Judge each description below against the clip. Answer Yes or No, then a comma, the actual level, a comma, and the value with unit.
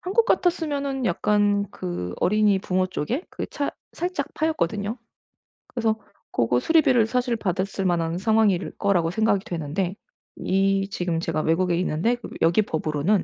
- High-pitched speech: Yes, high, 200 Hz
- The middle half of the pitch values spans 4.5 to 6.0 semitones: Yes, wide, 5.5 semitones